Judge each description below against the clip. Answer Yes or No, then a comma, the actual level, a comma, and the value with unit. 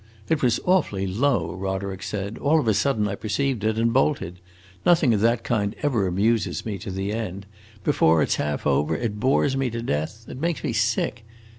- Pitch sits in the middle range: No, low, 110 Hz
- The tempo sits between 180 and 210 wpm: Yes, average, 200 wpm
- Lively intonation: No, average, 4.5 semitones